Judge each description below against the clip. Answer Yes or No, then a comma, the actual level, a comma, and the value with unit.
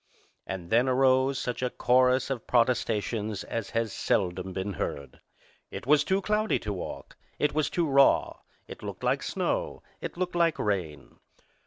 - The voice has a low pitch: Yes, low, 125 Hz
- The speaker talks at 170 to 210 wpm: No, average, 160 wpm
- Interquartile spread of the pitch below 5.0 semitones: No, average, 5.3 semitones